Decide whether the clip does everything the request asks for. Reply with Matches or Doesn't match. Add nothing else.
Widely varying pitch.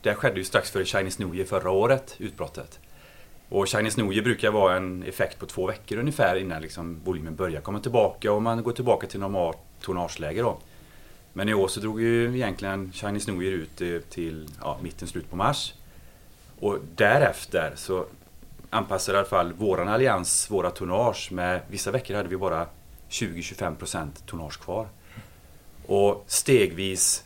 Doesn't match